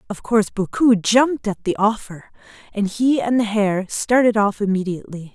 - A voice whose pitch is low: No, high, 210 Hz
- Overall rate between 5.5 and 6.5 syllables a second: No, 5.1 syllables/s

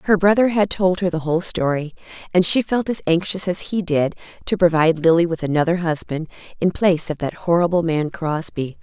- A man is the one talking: No, female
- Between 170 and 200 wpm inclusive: Yes, average, 195 wpm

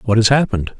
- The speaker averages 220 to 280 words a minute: Yes, fast, 225 wpm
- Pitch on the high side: No, low, 115 Hz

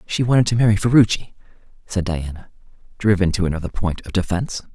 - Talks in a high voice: No, low, 100 Hz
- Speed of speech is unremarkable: Yes, average, 165 wpm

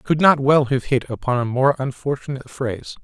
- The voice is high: No, low, 130 Hz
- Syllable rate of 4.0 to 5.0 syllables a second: No, 6.1 syllables/s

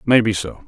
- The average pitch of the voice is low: Yes, low, 115 Hz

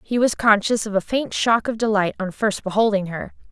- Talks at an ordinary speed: No, fast, 220 wpm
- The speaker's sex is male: No, female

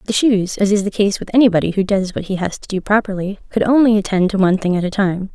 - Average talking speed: No, fast, 280 wpm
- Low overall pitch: No, high, 200 Hz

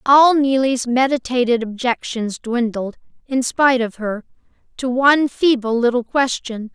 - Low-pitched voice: No, very high, 250 Hz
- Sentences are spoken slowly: Yes, slow, 125 wpm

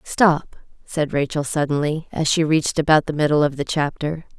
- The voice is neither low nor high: Yes, medium, 150 Hz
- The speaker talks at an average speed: Yes, average, 180 wpm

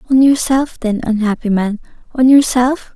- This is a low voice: No, high, 245 Hz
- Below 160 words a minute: Yes, average, 140 wpm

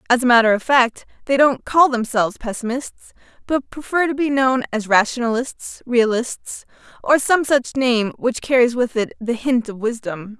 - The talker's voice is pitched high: Yes, high, 245 Hz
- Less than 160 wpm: No, average, 175 wpm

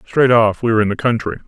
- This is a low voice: Yes, low, 115 Hz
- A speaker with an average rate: No, fast, 285 wpm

